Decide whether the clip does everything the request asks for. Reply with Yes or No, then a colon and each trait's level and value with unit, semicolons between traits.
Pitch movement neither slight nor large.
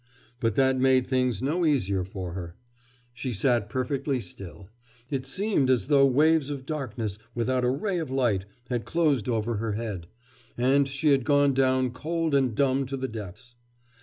Yes: average, 3.5 semitones